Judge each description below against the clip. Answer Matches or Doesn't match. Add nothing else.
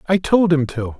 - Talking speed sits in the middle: Doesn't match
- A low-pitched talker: Doesn't match